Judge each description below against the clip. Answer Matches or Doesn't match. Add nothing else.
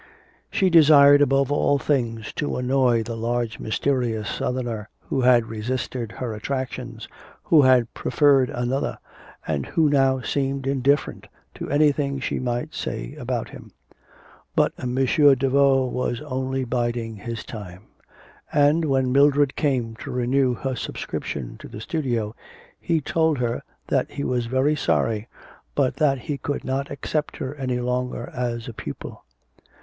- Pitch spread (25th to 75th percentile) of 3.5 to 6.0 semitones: Doesn't match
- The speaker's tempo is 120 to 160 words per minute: Matches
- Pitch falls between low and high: Doesn't match